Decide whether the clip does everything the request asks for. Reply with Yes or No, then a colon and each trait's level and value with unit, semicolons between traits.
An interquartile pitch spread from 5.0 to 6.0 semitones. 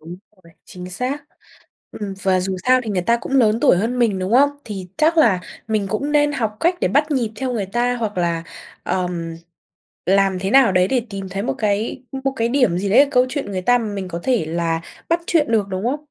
Yes: wide, 5.5 semitones